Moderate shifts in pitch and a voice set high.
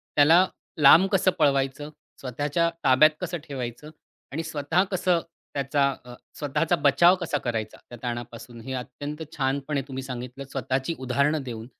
No: average, 3.5 semitones; medium, 140 Hz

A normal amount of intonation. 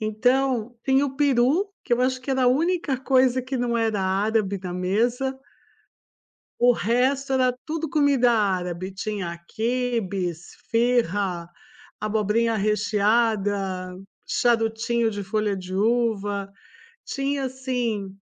Yes: average, 4.2 semitones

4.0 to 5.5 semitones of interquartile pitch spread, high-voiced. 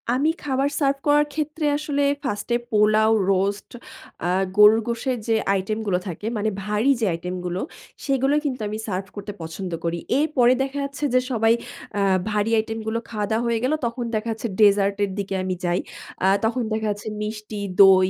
Yes: average, 4.3 semitones; high, 220 Hz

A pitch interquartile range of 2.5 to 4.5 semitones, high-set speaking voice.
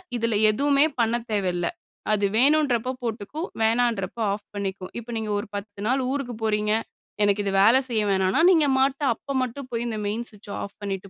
Yes: average, 3.7 semitones; high, 220 Hz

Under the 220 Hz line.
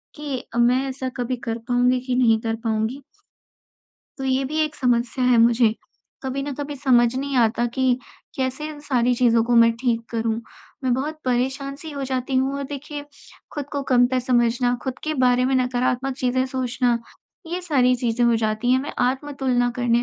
No: very high, 255 Hz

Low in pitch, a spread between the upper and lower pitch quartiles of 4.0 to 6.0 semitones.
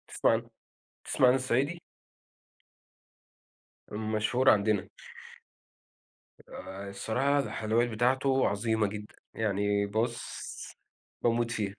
No: low, 110 Hz; average, 3.4 semitones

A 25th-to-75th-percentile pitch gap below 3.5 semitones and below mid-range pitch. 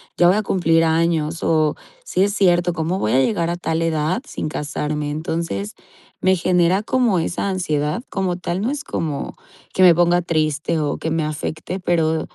No: average, 2.7 semitones; medium, 165 Hz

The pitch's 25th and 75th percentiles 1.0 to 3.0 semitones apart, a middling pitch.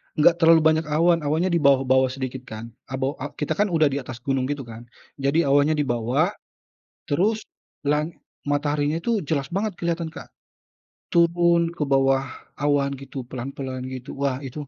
No: average, 3.6 semitones; medium, 145 Hz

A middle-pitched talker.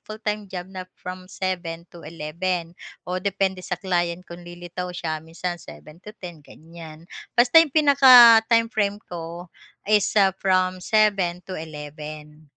Yes: medium, 180 Hz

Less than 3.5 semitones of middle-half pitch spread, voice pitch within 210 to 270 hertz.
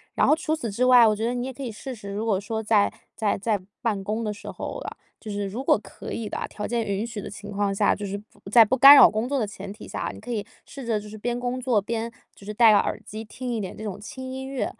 Yes: average, 2.9 semitones; high, 220 Hz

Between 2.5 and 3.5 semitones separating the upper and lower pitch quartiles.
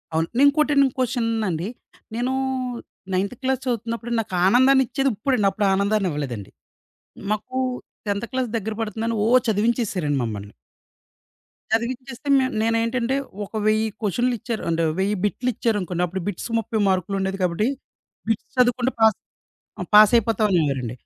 No: average, 4.2 semitones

